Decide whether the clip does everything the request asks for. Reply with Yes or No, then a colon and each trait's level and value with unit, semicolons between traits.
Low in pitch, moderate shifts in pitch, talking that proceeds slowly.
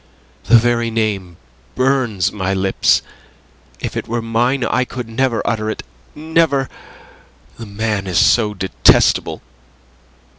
Yes: low, 115 Hz; average, 3.7 semitones; slow, 120 wpm